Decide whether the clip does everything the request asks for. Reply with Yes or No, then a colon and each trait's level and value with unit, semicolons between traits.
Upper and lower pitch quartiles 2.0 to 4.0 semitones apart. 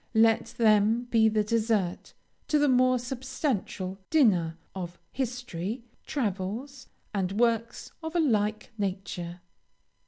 No: average, 4.5 semitones